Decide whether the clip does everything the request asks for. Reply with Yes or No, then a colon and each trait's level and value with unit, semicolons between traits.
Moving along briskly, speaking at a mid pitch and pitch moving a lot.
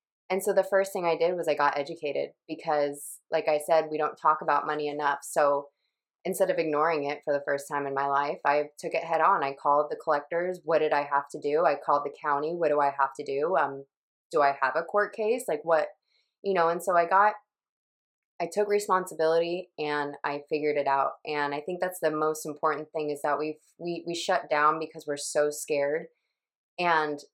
No: fast, 220 wpm; medium, 155 Hz; average, 2.9 semitones